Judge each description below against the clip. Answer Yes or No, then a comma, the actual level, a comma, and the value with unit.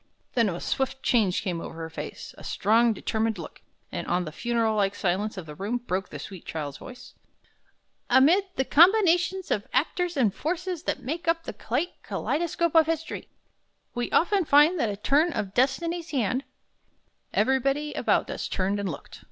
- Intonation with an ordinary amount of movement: No, wide, 8.5 semitones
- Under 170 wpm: No, average, 175 wpm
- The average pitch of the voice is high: Yes, very high, 250 Hz